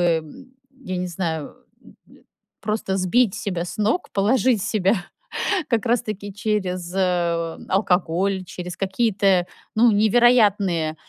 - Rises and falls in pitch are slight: No, average, 3.3 semitones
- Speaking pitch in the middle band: No, high, 195 Hz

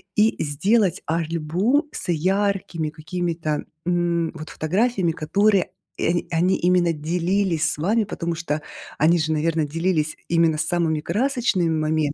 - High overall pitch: No, medium, 170 Hz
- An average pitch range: Yes, average, 3.2 semitones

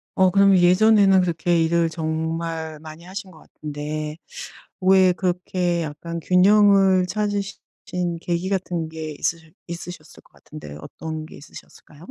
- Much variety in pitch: No, average, 2.8 semitones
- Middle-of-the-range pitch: Yes, medium, 170 Hz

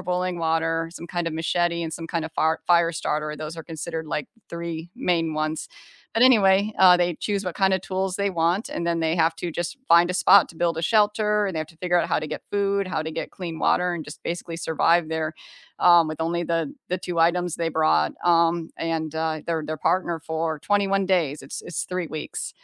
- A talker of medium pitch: Yes, medium, 170 Hz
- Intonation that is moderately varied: No, narrow, 2.0 semitones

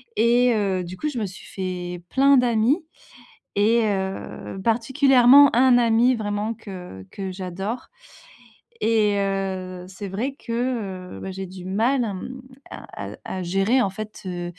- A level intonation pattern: No, average, 4.4 semitones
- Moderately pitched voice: No, high, 210 Hz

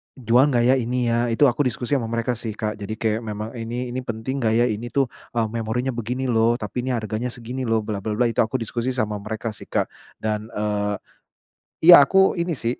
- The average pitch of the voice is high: No, low, 115 Hz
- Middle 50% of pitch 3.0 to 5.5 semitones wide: No, narrow, 2.4 semitones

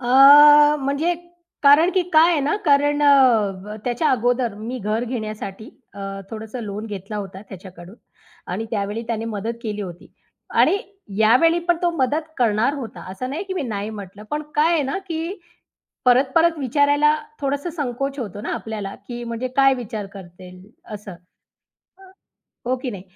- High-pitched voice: Yes, high, 240 Hz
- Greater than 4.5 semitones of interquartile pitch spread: Yes, wide, 5.5 semitones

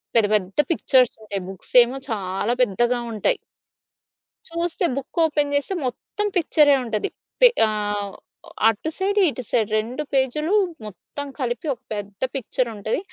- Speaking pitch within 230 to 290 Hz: Yes, high, 245 Hz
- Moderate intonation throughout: No, wide, 5.8 semitones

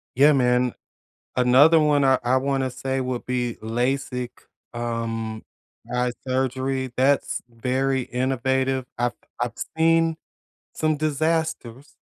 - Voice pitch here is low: Yes, low, 130 Hz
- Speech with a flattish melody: Yes, narrow, 2.0 semitones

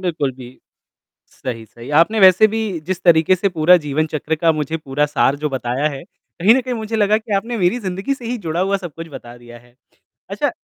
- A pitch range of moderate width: No, wide, 5.7 semitones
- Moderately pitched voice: Yes, medium, 165 Hz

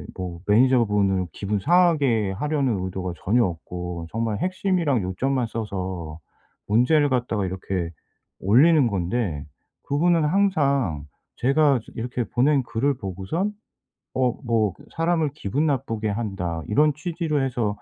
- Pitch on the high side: No, low, 120 Hz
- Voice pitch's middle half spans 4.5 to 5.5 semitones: No, wide, 7.1 semitones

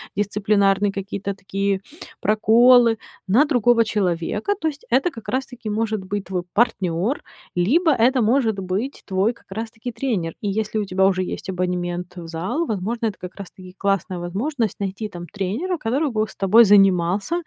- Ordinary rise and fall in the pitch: Yes, average, 3.8 semitones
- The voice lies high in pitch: Yes, high, 205 Hz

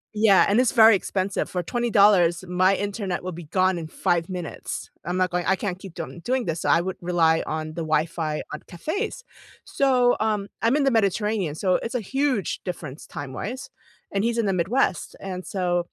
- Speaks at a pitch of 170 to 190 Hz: Yes, medium, 185 Hz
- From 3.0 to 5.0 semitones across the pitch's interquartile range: Yes, average, 4.2 semitones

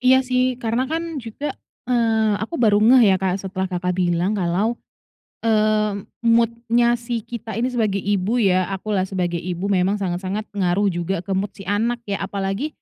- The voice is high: Yes, high, 205 Hz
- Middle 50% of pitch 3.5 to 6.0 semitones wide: Yes, average, 3.8 semitones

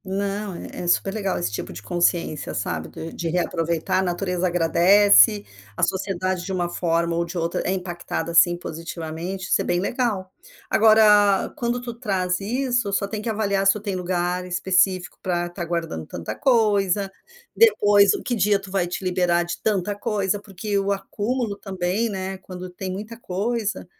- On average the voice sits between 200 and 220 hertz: No, high, 190 Hz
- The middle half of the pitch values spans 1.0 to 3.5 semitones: Yes, average, 2.8 semitones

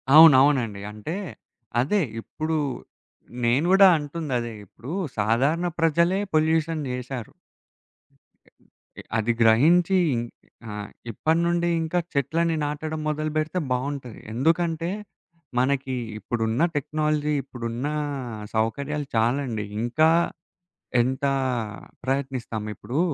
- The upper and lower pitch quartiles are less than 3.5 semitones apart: No, average, 4.9 semitones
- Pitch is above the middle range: No, medium, 145 Hz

